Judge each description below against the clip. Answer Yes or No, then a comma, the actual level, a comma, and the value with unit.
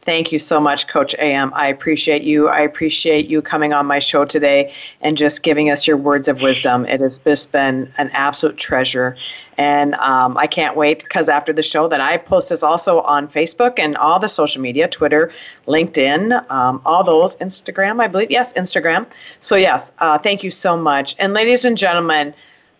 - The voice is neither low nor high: Yes, medium, 150 Hz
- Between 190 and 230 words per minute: Yes, average, 195 wpm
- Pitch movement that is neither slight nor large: No, narrow, 2.2 semitones